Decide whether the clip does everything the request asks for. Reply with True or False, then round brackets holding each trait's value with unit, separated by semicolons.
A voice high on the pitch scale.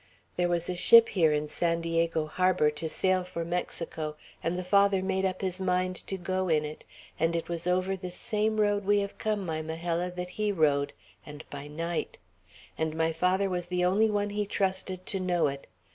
False (180 Hz)